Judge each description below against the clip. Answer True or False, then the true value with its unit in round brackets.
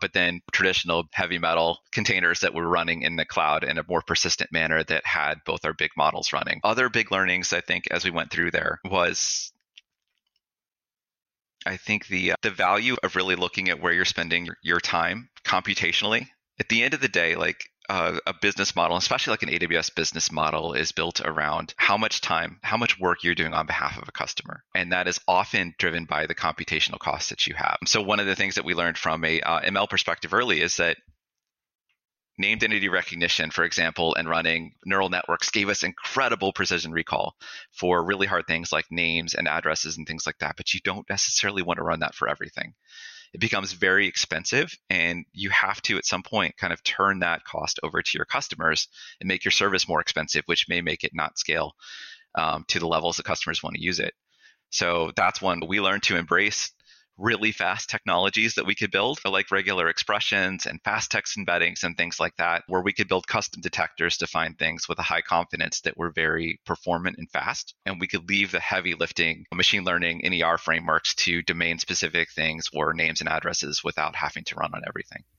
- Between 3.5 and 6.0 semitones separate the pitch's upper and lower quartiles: False (2.6 semitones)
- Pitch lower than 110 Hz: True (90 Hz)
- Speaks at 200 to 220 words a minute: True (205 wpm)